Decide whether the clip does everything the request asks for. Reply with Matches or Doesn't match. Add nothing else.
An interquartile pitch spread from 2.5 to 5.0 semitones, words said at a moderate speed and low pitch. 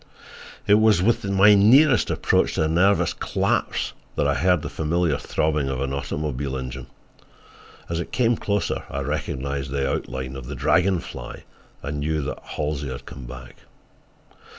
Doesn't match